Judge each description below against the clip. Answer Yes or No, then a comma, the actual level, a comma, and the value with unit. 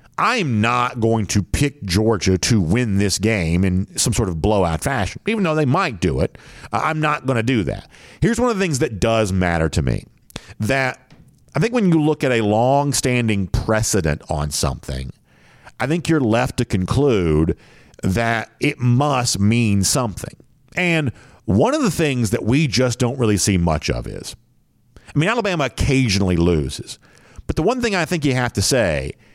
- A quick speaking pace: No, average, 185 wpm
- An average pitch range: No, wide, 6.6 semitones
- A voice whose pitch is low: Yes, low, 120 Hz